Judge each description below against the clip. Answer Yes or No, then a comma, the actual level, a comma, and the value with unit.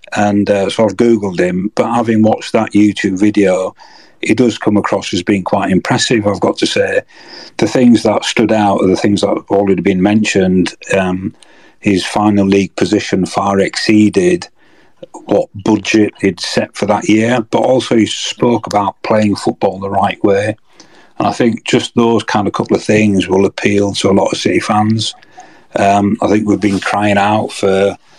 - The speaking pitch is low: Yes, low, 105 Hz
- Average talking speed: Yes, average, 190 wpm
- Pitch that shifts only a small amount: Yes, narrow, 1.8 semitones